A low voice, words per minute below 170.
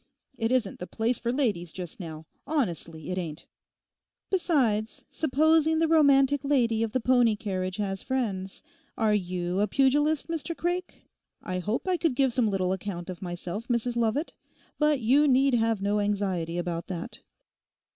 No: high, 225 Hz; average, 155 wpm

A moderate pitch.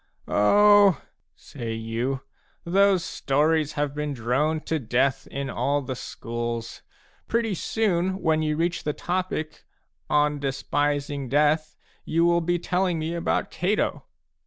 Yes: medium, 150 Hz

